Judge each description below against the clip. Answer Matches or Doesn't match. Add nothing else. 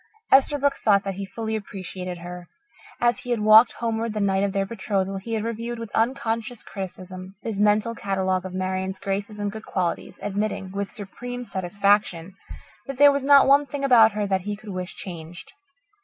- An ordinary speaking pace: Matches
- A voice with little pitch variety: Doesn't match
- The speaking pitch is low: Doesn't match